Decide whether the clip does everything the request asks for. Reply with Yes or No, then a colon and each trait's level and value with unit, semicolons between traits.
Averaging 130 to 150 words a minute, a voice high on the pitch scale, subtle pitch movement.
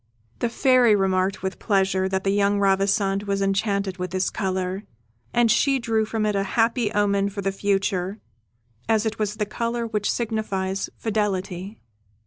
No: average, 160 wpm; high, 200 Hz; narrow, 2.1 semitones